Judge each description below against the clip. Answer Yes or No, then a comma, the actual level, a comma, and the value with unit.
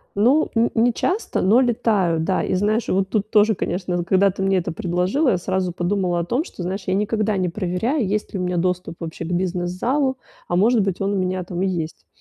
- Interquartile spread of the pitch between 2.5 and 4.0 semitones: Yes, average, 3.3 semitones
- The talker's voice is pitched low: No, high, 190 Hz